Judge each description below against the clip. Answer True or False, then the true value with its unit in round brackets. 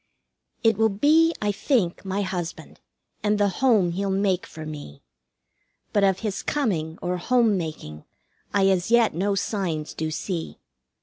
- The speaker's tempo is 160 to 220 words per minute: False (150 wpm)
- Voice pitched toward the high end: True (195 Hz)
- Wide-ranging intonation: False (3.7 semitones)